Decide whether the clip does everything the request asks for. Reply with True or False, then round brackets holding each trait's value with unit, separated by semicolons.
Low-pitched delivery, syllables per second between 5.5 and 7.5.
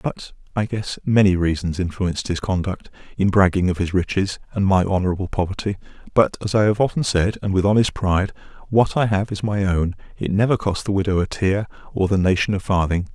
True (95 Hz; 5.8 syllables/s)